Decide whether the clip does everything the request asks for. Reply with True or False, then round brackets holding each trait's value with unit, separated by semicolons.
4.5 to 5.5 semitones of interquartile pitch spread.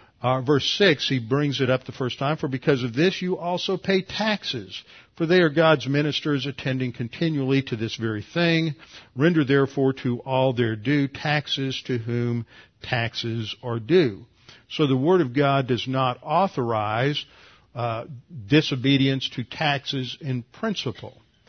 False (3.8 semitones)